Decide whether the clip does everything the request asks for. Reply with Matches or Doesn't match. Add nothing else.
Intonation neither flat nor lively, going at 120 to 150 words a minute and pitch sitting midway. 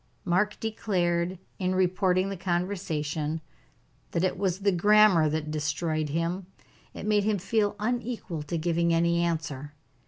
Matches